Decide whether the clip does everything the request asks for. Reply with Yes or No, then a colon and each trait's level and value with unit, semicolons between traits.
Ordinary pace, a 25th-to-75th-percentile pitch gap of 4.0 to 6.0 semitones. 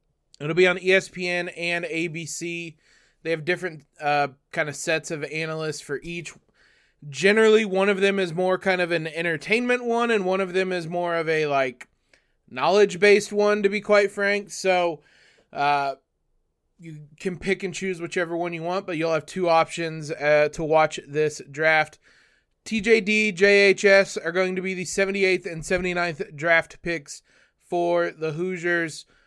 No: average, 165 wpm; average, 3.3 semitones